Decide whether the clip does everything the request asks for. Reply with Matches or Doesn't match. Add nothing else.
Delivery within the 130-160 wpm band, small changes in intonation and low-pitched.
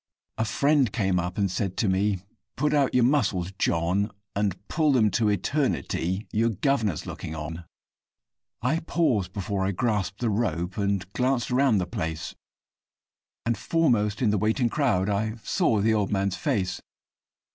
Doesn't match